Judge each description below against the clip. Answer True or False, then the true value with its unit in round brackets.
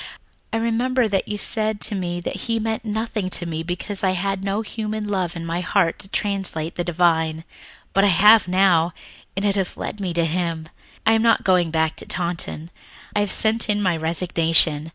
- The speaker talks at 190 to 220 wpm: True (200 wpm)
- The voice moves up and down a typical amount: True (3.8 semitones)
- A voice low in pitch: False (185 Hz)